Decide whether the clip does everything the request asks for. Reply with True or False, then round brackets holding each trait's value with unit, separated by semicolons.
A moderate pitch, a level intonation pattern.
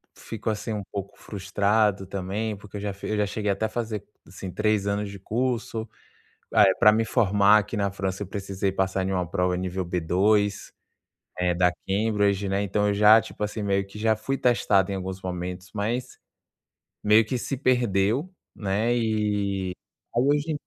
False (100 Hz; 2.2 semitones)